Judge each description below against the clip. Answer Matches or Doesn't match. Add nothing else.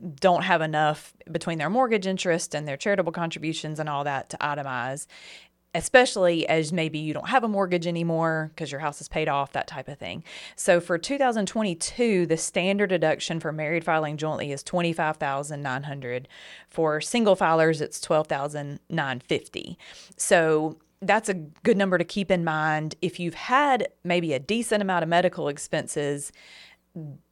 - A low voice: Doesn't match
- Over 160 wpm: Doesn't match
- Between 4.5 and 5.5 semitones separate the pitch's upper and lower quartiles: Doesn't match